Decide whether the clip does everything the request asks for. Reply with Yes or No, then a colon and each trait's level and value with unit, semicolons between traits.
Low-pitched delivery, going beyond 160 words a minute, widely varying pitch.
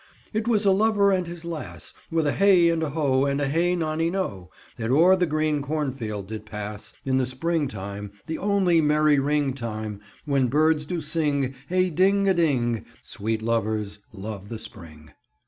No: medium, 145 Hz; average, 180 wpm; wide, 7.3 semitones